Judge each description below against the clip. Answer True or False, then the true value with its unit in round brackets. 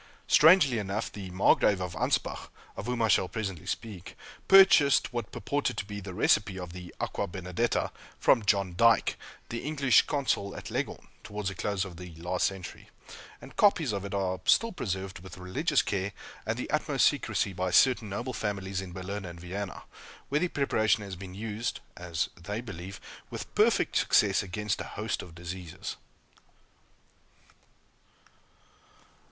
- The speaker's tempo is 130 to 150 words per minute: False (160 wpm)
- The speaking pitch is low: True (100 Hz)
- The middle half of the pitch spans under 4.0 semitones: True (3.6 semitones)